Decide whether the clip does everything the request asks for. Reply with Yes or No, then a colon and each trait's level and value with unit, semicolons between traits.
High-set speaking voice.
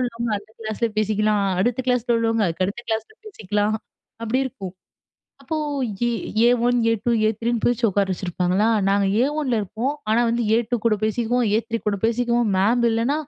Yes: high, 225 Hz